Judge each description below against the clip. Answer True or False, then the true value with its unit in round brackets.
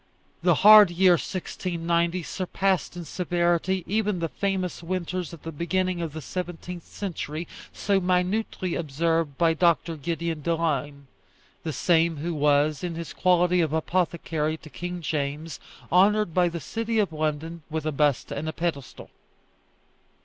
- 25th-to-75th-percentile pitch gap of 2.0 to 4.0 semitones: True (2.5 semitones)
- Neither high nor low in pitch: True (170 Hz)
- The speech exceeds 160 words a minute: False (145 wpm)